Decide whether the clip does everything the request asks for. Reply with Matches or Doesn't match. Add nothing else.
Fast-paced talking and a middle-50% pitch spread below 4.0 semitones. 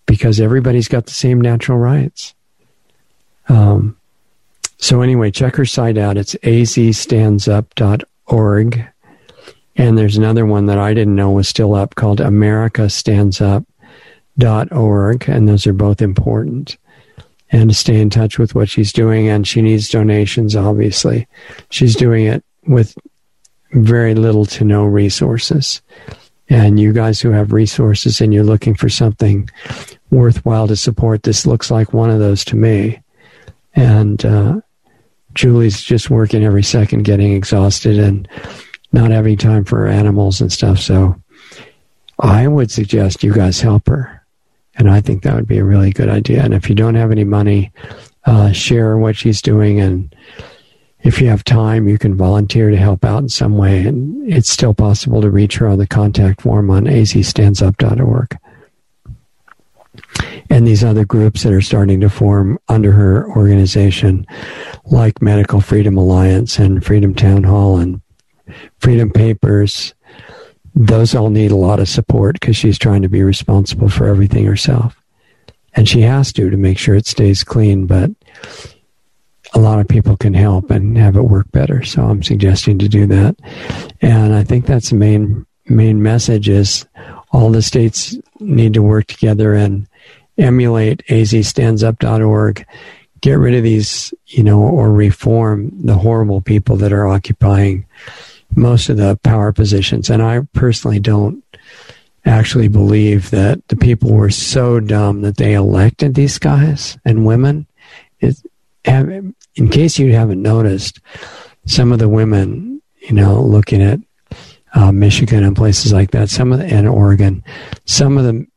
Doesn't match